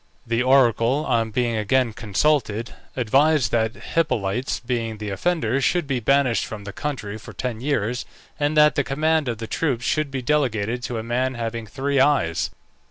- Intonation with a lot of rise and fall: No, average, 3.9 semitones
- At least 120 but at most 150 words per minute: No, average, 170 wpm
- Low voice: Yes, low, 125 Hz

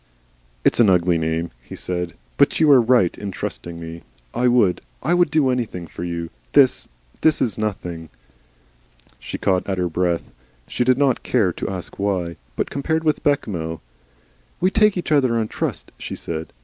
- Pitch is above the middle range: No, low, 100 Hz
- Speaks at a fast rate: No, average, 175 wpm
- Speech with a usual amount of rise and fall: No, wide, 7.1 semitones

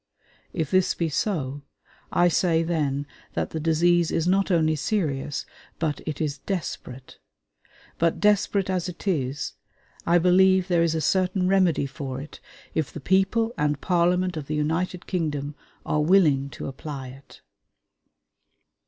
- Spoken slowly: No, average, 145 wpm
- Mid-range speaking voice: Yes, medium, 165 Hz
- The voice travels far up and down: No, average, 3.9 semitones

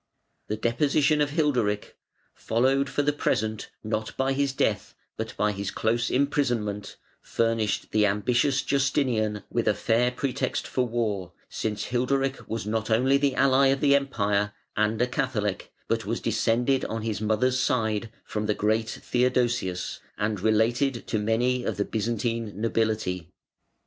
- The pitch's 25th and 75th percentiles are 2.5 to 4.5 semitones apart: Yes, average, 3.5 semitones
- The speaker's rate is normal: Yes, average, 150 wpm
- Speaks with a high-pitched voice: No, low, 115 Hz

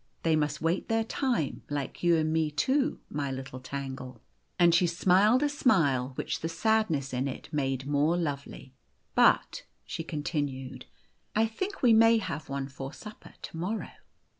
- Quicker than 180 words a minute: No, average, 175 wpm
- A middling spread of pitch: No, wide, 7.5 semitones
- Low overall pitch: No, medium, 160 Hz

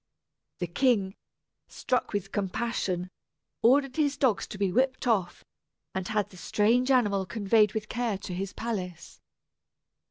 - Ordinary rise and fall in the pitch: Yes, average, 4.3 semitones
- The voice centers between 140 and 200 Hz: No, high, 210 Hz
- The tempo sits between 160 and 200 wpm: No, slow, 135 wpm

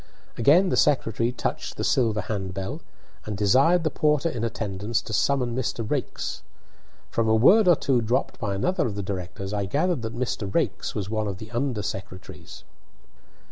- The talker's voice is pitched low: Yes, low, 115 Hz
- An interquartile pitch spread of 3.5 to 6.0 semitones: Yes, average, 4.9 semitones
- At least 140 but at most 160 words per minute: No, average, 175 wpm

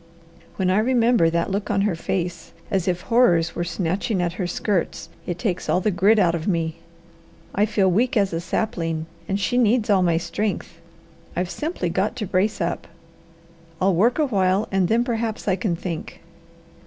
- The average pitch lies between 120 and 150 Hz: No, high, 190 Hz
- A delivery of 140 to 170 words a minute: No, average, 185 wpm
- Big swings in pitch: No, average, 3.8 semitones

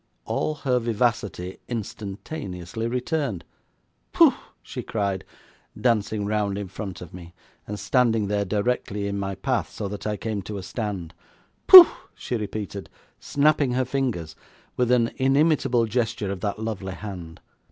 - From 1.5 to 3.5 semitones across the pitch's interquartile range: No, average, 3.9 semitones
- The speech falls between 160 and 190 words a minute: No, average, 140 wpm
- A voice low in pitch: Yes, low, 105 Hz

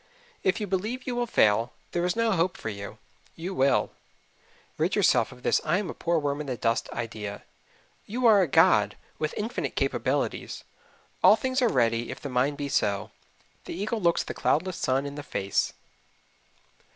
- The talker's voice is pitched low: No, medium, 155 Hz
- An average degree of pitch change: No, wide, 8.4 semitones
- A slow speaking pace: No, average, 185 wpm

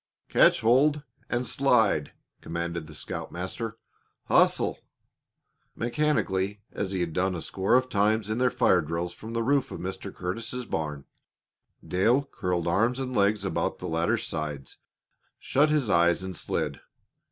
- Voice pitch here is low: Yes, low, 100 Hz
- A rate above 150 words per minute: No, average, 145 wpm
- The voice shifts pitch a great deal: Yes, wide, 6.0 semitones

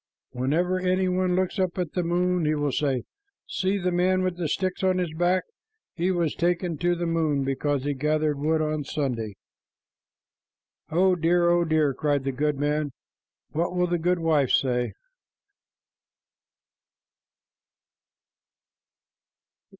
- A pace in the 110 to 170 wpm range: Yes, slow, 135 wpm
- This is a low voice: No, medium, 165 Hz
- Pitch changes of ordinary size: Yes, average, 3.5 semitones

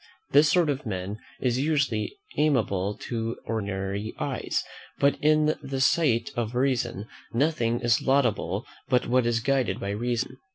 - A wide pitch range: No, average, 3.9 semitones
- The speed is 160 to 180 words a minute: No, average, 140 wpm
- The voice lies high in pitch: No, low, 120 Hz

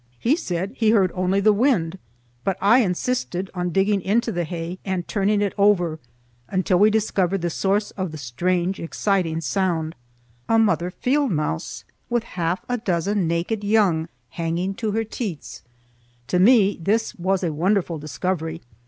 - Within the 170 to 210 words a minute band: No, average, 155 wpm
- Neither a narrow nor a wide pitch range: Yes, average, 3.6 semitones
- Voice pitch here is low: No, medium, 185 Hz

